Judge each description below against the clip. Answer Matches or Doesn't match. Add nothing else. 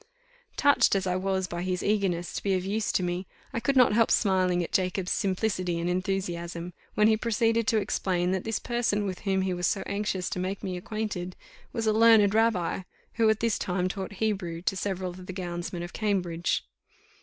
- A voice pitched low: Doesn't match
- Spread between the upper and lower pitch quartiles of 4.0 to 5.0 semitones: Doesn't match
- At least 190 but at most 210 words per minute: Matches